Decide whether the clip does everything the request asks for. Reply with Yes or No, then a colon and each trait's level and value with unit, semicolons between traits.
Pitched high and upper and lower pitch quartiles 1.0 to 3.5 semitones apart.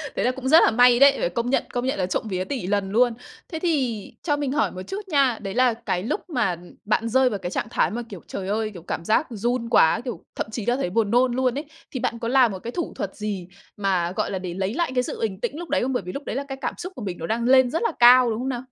No: high, 240 Hz; average, 4.8 semitones